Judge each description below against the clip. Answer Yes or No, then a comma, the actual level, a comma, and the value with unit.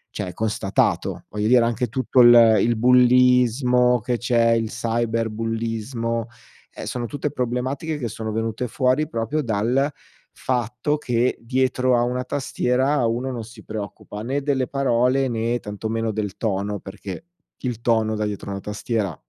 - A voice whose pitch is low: Yes, low, 120 Hz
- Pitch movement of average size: No, narrow, 2.3 semitones